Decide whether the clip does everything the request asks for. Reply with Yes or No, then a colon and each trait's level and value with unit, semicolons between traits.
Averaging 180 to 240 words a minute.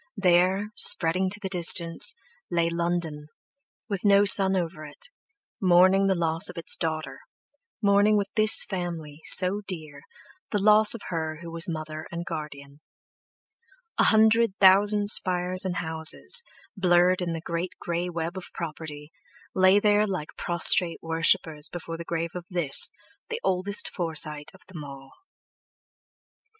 No: average, 140 wpm